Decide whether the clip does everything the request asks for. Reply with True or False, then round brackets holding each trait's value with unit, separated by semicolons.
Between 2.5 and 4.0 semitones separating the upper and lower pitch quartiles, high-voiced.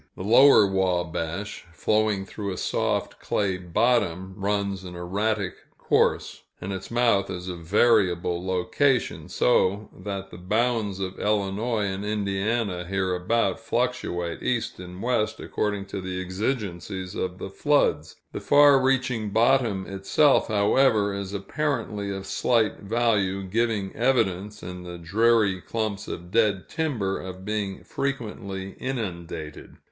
False (3.5 semitones; 100 Hz)